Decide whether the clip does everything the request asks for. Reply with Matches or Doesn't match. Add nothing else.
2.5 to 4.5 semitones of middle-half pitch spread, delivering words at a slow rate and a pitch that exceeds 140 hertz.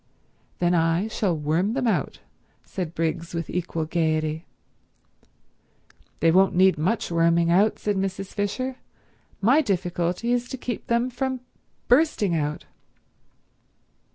Doesn't match